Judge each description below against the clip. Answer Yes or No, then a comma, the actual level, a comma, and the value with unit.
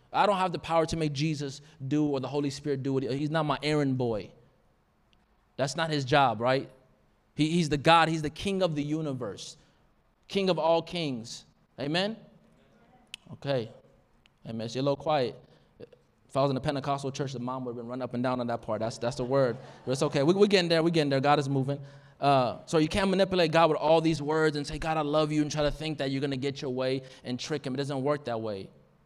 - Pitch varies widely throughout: No, average, 3.1 semitones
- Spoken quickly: Yes, fast, 245 wpm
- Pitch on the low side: No, medium, 145 Hz